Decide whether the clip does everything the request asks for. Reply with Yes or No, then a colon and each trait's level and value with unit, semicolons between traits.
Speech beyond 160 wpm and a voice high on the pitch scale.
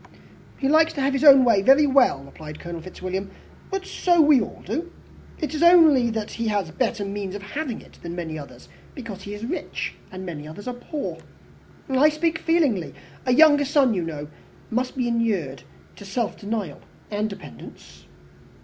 Yes: average, 180 wpm; high, 230 Hz